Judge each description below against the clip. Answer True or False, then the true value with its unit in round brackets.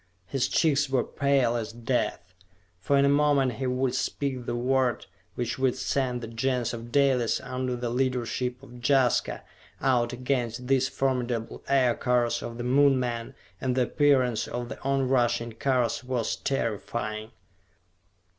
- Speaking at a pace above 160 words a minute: False (150 wpm)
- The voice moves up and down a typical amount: False (2.0 semitones)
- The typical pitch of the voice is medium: False (125 Hz)